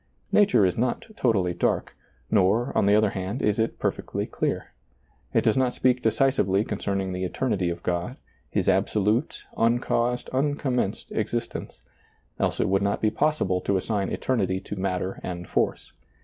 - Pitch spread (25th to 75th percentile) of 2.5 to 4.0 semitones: No, average, 4.5 semitones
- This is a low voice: Yes, low, 105 Hz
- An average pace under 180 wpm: Yes, average, 165 wpm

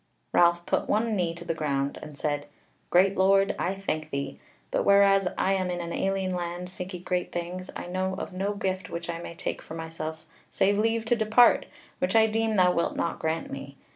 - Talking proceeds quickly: Yes, fast, 210 wpm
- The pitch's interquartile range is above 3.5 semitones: No, average, 2.7 semitones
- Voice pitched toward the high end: No, medium, 180 Hz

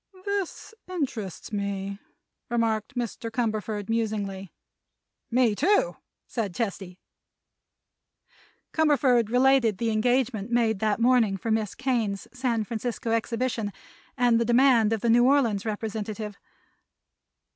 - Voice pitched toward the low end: No, high, 230 Hz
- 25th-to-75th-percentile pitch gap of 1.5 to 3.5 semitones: Yes, average, 2.9 semitones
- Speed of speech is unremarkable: No, slow, 110 wpm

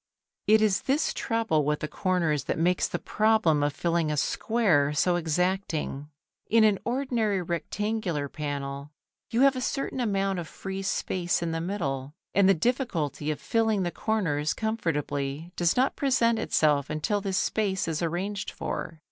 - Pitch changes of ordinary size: No, wide, 6.2 semitones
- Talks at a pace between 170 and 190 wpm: No, average, 160 wpm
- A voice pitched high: No, medium, 180 Hz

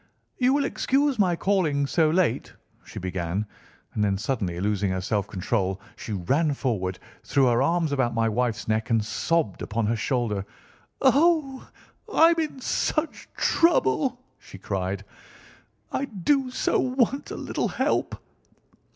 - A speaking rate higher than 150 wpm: No, average, 140 wpm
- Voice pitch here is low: Yes, low, 130 Hz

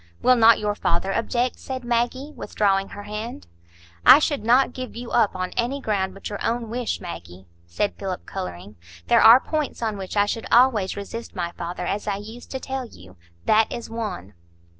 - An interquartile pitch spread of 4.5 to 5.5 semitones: No, average, 3.9 semitones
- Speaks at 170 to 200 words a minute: Yes, average, 190 wpm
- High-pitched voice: Yes, high, 220 Hz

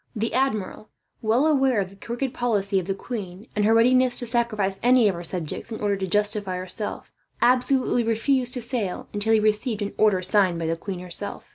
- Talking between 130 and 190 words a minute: No, fast, 205 wpm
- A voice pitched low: No, high, 215 Hz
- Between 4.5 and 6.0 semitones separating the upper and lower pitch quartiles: No, average, 3.8 semitones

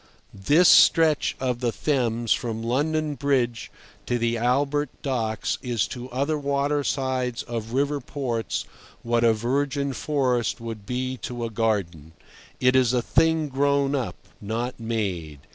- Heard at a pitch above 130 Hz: No, low, 125 Hz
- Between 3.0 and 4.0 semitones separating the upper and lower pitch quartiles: Yes, average, 3.4 semitones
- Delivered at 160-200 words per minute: No, average, 140 wpm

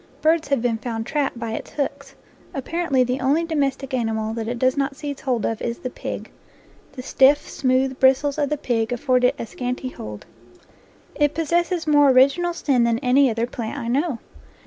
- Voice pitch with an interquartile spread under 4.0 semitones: Yes, average, 3.3 semitones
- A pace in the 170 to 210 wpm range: Yes, average, 190 wpm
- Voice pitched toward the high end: Yes, very high, 265 Hz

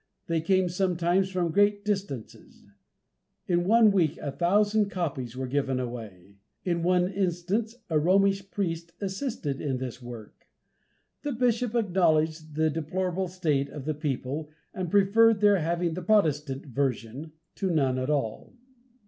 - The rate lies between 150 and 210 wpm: No, average, 140 wpm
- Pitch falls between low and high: Yes, medium, 170 Hz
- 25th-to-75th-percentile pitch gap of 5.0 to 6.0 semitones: Yes, wide, 5.4 semitones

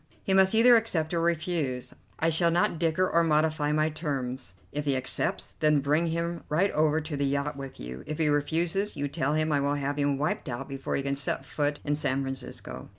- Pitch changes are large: No, average, 3.0 semitones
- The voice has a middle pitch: Yes, medium, 150 Hz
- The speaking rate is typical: No, fast, 215 wpm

